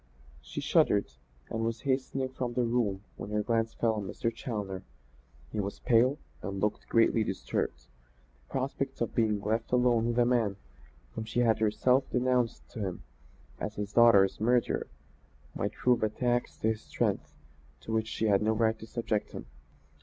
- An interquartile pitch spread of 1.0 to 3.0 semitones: Yes, narrow, 2.5 semitones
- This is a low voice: Yes, low, 115 Hz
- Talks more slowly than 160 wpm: No, average, 175 wpm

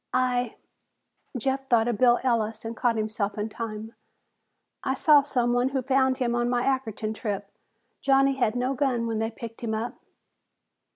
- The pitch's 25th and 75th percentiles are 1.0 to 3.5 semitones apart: Yes, average, 2.9 semitones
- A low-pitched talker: No, high, 240 Hz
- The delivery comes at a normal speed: Yes, average, 170 wpm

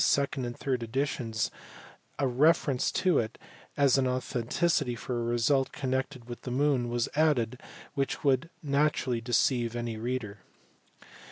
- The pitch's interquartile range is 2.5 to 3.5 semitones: Yes, average, 2.8 semitones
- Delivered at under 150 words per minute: Yes, average, 140 wpm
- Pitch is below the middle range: Yes, low, 130 Hz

